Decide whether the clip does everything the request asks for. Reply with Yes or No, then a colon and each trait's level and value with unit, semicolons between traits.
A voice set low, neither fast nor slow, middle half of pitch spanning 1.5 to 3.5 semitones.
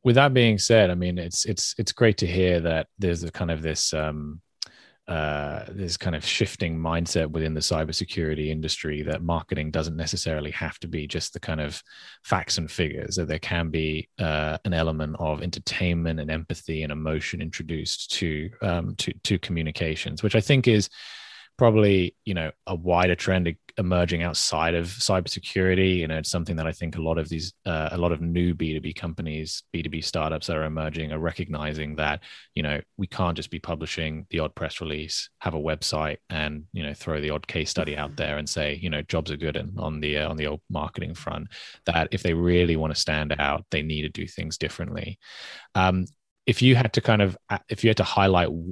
No: very low, 85 Hz; fast, 210 wpm; average, 2.8 semitones